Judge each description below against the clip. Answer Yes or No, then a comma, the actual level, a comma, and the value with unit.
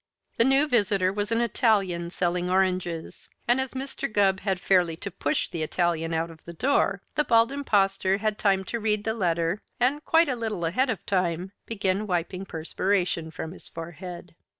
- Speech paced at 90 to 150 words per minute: No, average, 180 wpm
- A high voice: Yes, high, 195 Hz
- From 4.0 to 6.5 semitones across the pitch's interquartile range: Yes, average, 4.5 semitones